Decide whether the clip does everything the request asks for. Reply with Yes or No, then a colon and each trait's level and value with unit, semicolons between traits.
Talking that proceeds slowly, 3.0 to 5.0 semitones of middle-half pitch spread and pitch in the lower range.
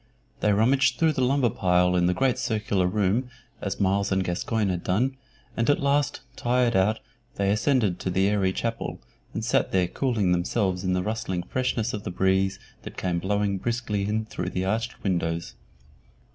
No: average, 180 wpm; average, 4.2 semitones; low, 100 Hz